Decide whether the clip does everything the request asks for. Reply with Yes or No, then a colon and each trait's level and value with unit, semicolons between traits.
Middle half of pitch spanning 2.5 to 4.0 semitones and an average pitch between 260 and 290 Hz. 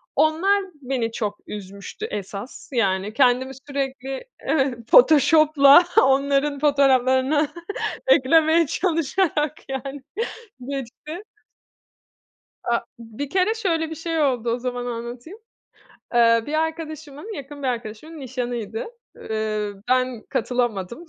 No: average, 4.5 semitones; very high, 270 Hz